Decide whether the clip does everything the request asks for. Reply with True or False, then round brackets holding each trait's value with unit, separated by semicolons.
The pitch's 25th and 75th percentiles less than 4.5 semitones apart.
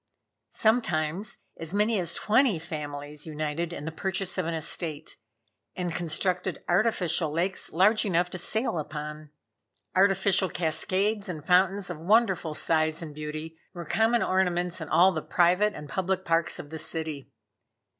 True (3.4 semitones)